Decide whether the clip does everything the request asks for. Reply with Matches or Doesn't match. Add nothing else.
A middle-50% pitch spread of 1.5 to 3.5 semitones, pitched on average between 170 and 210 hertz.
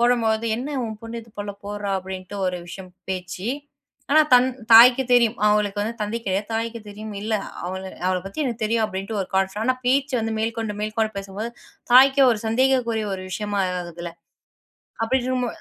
Doesn't match